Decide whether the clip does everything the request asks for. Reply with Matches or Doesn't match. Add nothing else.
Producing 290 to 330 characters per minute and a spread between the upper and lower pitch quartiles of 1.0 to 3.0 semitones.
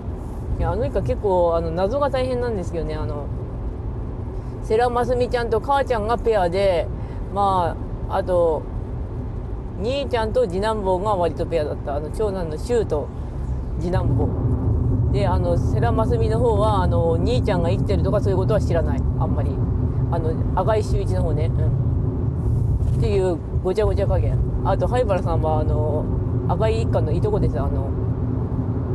Matches